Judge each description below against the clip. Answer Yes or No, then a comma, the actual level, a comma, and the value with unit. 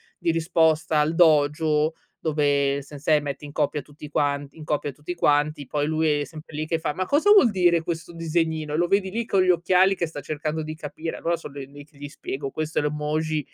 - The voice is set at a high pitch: No, medium, 155 Hz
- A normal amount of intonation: No, narrow, 2.1 semitones